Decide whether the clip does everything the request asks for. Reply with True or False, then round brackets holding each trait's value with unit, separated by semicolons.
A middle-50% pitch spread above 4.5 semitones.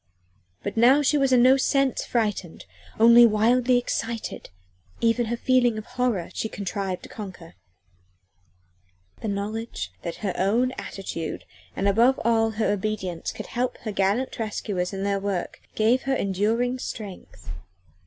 False (3.7 semitones)